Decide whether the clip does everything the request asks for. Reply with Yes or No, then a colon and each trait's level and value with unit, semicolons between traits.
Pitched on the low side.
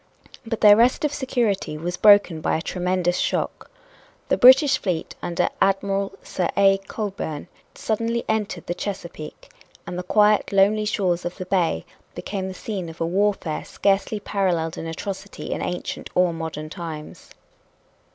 No: high, 195 Hz